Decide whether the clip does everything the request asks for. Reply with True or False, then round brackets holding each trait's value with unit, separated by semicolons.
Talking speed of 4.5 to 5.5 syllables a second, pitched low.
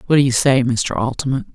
False (5.9 syllables/s; 130 Hz)